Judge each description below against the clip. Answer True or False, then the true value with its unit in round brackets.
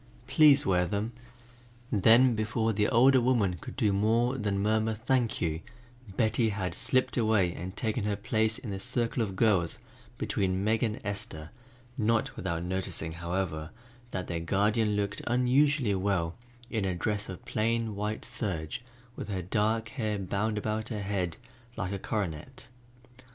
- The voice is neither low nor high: False (105 Hz)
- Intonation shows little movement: False (3.2 semitones)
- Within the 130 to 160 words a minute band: True (155 wpm)